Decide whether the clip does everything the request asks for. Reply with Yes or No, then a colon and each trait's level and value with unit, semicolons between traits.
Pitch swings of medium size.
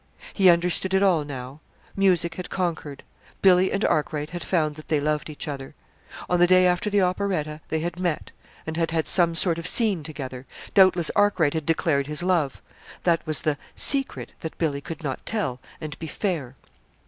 Yes: average, 3.3 semitones